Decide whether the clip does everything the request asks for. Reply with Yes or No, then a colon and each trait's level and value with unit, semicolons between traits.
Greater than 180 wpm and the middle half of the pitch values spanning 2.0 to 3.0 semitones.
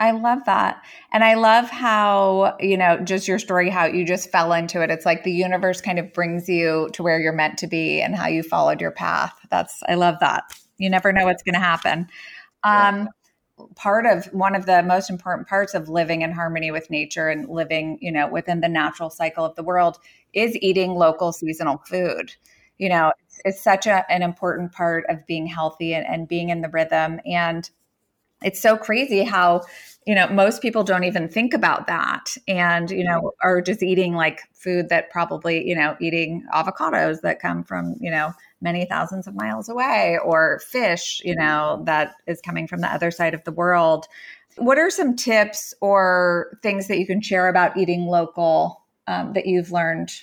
Yes: average, 200 wpm; average, 2.7 semitones